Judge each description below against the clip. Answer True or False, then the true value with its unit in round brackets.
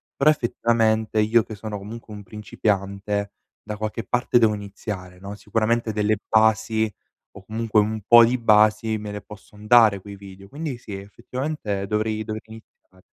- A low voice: True (110 Hz)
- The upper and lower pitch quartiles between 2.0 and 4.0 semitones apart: False (1.6 semitones)